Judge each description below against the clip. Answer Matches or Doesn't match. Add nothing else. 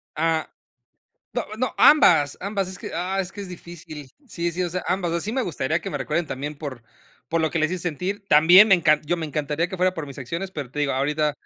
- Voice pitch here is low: Doesn't match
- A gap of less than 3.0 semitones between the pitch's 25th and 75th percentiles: Doesn't match